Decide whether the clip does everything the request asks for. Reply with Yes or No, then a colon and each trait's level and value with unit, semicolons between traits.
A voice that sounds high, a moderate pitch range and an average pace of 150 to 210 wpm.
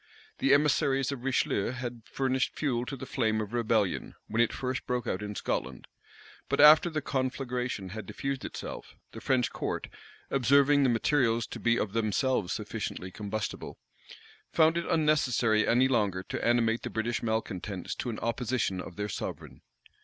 No: low, 120 Hz; average, 3.6 semitones; average, 160 wpm